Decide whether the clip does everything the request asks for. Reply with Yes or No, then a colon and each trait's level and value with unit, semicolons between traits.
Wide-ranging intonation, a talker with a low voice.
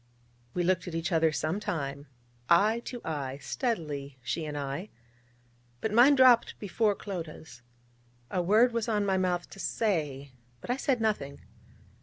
No: wide, 6.7 semitones; medium, 180 Hz